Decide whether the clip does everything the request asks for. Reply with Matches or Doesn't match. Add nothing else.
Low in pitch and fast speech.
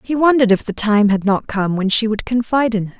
Doesn't match